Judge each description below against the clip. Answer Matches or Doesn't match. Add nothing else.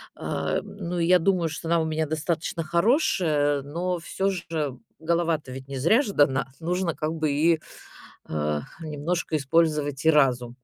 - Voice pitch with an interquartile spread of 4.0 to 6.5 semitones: Doesn't match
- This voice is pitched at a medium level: Matches